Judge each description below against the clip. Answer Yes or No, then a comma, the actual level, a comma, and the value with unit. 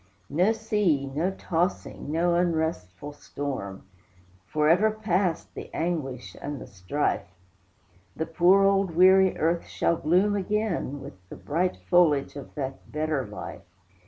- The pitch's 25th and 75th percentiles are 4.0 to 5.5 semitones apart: Yes, average, 4.4 semitones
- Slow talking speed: Yes, slow, 130 wpm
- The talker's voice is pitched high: No, medium, 165 Hz